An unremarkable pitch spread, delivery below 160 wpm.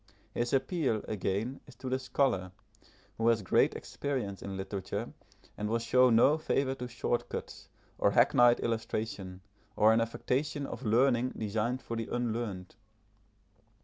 Yes: average, 3.3 semitones; average, 145 wpm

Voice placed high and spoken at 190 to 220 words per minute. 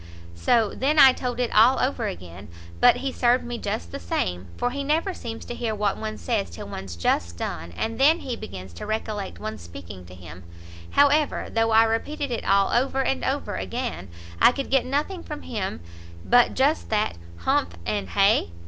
Yes: high, 225 Hz; average, 195 wpm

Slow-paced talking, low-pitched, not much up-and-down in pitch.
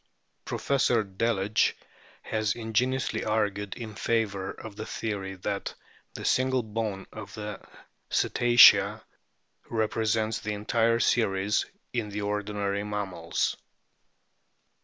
Yes: slow, 100 wpm; low, 105 Hz; narrow, 2.0 semitones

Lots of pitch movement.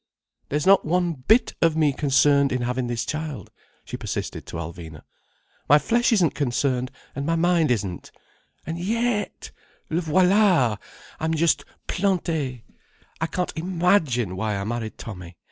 Yes: wide, 6.4 semitones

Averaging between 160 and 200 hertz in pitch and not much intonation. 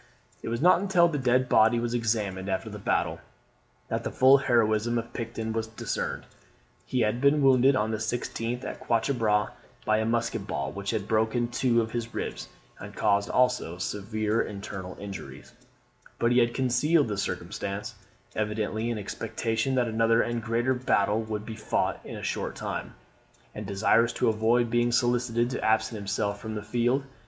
No: low, 115 Hz; narrow, 2.3 semitones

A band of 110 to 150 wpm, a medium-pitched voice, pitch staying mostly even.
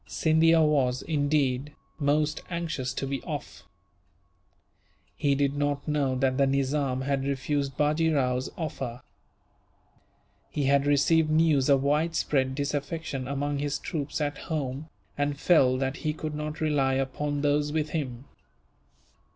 Yes: slow, 135 wpm; medium, 145 Hz; narrow, 2.0 semitones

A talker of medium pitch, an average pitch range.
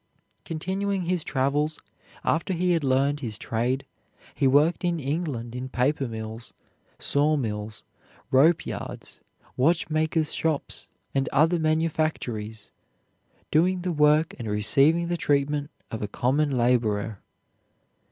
Yes: medium, 145 Hz; average, 4.7 semitones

